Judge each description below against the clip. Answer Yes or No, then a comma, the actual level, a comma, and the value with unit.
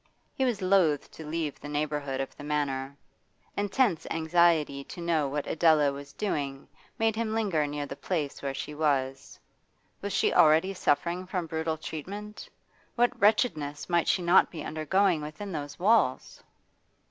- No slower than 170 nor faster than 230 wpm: No, average, 155 wpm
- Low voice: No, medium, 160 Hz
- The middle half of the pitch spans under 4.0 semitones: No, average, 4.6 semitones